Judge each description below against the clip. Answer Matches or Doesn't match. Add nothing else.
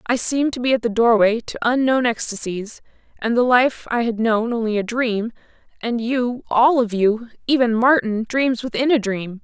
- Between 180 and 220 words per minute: Doesn't match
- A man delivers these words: Doesn't match